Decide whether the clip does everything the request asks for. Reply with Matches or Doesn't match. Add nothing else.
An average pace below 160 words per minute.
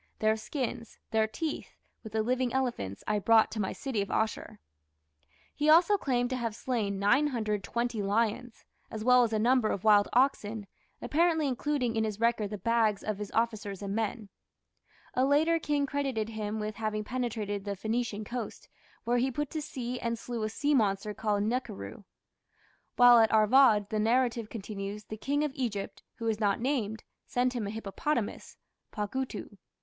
Doesn't match